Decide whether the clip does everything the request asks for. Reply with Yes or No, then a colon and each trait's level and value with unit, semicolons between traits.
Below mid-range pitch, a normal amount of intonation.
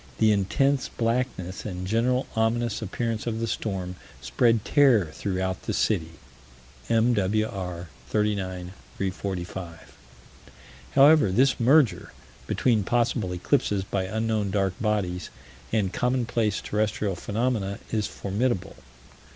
Yes: low, 105 Hz; average, 3.8 semitones